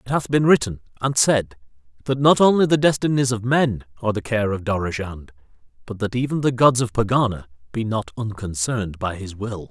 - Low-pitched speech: Yes, low, 115 Hz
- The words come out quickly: No, average, 190 wpm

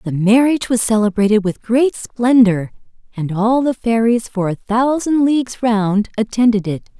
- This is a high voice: Yes, high, 225 Hz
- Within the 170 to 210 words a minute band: No, average, 155 wpm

